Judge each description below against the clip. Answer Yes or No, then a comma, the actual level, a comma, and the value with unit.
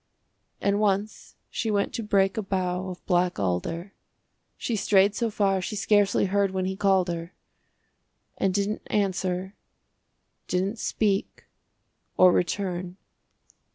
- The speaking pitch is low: No, high, 195 Hz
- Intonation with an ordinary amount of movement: No, narrow, 1.9 semitones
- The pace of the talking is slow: Yes, slow, 125 wpm